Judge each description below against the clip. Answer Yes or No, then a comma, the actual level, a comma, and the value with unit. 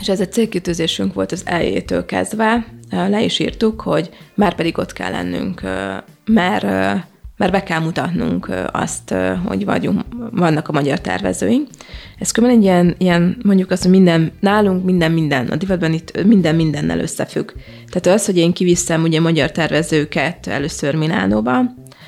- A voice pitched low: No, medium, 165 Hz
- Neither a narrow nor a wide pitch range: No, wide, 5.8 semitones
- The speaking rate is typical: No, fast, 160 wpm